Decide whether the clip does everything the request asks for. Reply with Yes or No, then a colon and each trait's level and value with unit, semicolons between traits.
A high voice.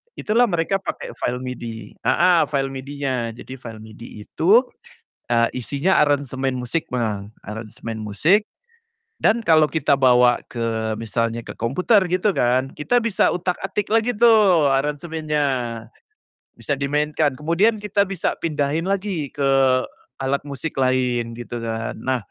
No: medium, 140 Hz